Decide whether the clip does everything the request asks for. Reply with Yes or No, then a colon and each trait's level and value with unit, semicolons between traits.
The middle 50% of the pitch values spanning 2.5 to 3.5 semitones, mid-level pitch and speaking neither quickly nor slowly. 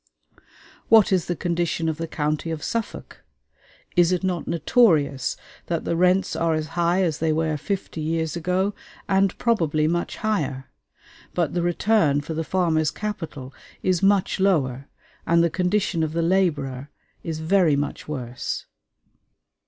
Yes: average, 3.2 semitones; medium, 165 Hz; average, 150 wpm